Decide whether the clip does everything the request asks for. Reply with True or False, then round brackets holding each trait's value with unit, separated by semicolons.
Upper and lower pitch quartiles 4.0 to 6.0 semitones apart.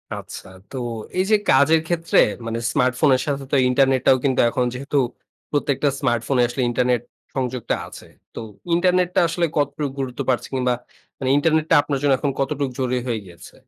False (2.6 semitones)